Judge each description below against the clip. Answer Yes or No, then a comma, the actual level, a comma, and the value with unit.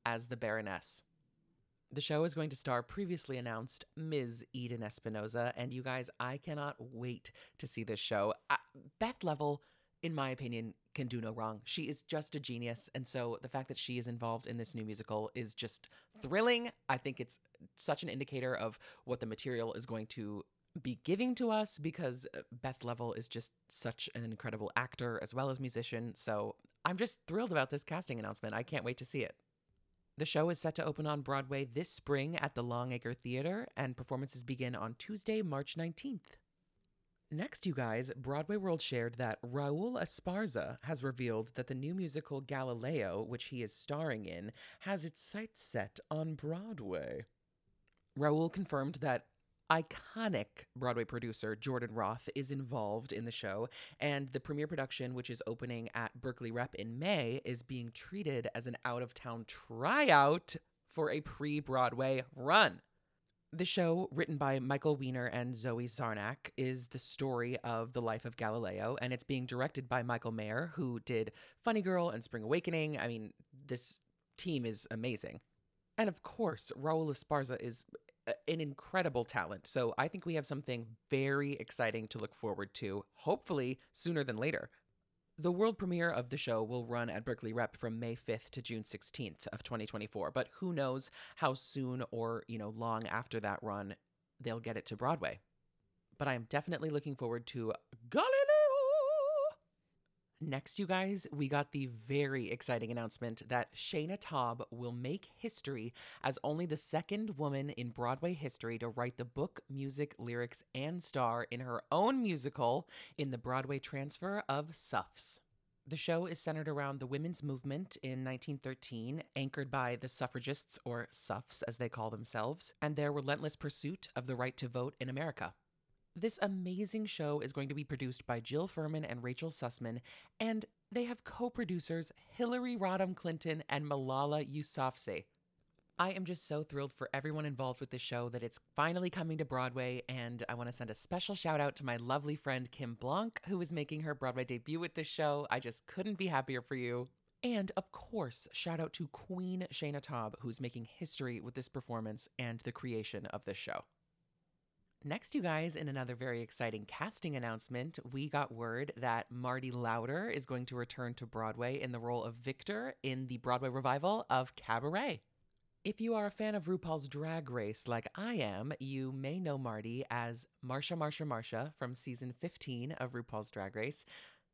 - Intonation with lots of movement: No, average, 4.5 semitones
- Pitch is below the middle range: Yes, low, 130 Hz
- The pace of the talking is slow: No, average, 180 wpm